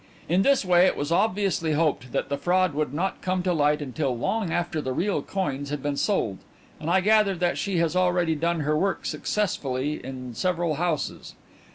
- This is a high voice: No, medium, 170 Hz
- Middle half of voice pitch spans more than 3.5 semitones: Yes, average, 4.1 semitones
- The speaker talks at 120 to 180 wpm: No, average, 195 wpm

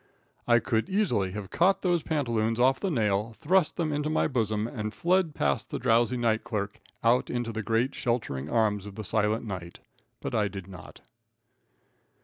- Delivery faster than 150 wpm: Yes, average, 175 wpm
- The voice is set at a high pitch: No, low, 115 Hz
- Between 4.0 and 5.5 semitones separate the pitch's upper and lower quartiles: Yes, average, 4.3 semitones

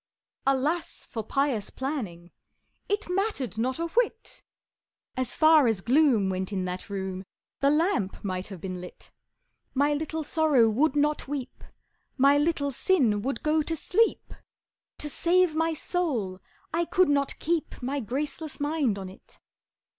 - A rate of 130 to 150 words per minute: Yes, average, 145 wpm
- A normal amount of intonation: No, wide, 6.7 semitones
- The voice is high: Yes, very high, 280 Hz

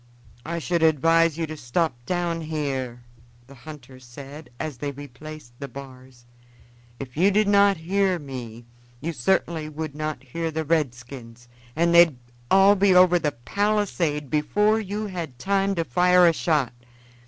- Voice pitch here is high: No, medium, 155 Hz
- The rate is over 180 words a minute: No, average, 155 wpm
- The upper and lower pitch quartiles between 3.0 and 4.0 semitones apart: No, average, 4.8 semitones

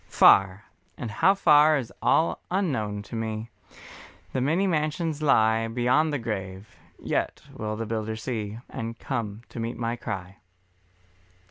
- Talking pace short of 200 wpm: Yes, average, 140 wpm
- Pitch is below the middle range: Yes, low, 115 Hz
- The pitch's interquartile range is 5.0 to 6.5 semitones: Yes, wide, 5.5 semitones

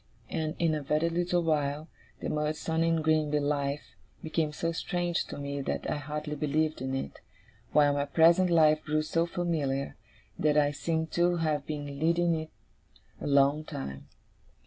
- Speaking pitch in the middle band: Yes, medium, 155 Hz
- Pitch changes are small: Yes, narrow, 2.3 semitones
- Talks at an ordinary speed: Yes, average, 165 wpm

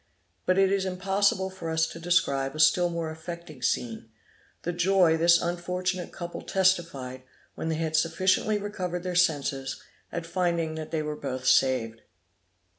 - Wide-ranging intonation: No, average, 2.8 semitones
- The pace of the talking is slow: No, average, 155 wpm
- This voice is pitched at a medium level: Yes, medium, 170 Hz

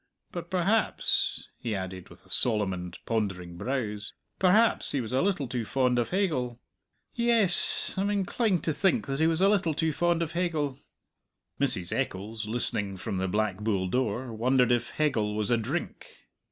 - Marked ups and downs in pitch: Yes, wide, 8.5 semitones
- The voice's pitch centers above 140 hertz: No, low, 125 Hz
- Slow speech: No, average, 170 wpm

